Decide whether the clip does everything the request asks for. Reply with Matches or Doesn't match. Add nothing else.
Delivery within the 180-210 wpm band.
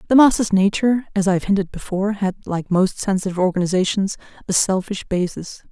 Doesn't match